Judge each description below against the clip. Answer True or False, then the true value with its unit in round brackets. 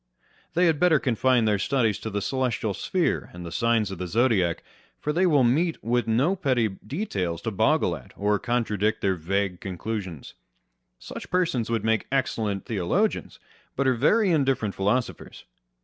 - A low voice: True (115 Hz)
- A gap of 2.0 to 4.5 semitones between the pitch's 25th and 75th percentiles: False (5.4 semitones)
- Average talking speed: True (165 wpm)